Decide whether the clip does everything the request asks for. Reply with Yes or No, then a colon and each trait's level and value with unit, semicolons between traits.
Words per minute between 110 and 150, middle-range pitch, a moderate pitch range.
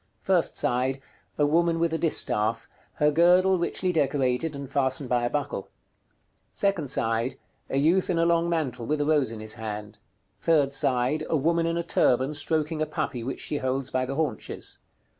No: average, 180 wpm; medium, 145 Hz; average, 4.4 semitones